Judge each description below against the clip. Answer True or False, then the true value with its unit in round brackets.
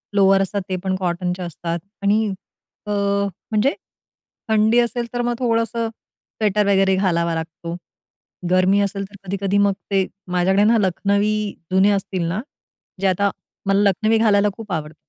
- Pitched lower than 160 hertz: False (200 Hz)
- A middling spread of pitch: False (2.3 semitones)